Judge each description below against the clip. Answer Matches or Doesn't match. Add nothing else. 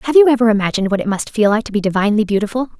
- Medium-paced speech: Doesn't match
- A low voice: Doesn't match